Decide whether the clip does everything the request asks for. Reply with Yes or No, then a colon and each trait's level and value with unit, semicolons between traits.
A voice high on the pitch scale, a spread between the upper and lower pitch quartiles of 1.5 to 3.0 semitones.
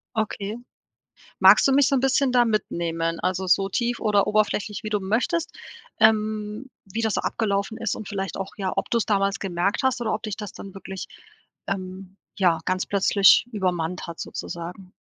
Yes: high, 205 Hz; average, 2.7 semitones